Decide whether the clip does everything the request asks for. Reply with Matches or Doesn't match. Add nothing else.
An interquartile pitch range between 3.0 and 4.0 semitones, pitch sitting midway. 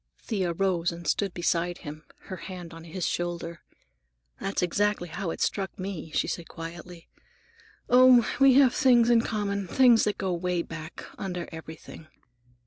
Matches